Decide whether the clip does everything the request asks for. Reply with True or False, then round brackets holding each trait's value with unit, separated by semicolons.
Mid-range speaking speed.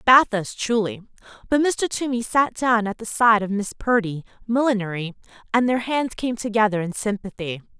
True (160 wpm)